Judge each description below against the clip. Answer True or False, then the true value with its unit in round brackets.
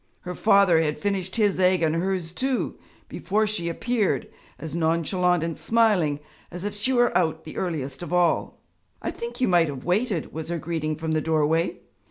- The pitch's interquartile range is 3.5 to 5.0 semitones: True (3.8 semitones)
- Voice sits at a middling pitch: True (175 Hz)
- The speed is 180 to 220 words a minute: True (185 wpm)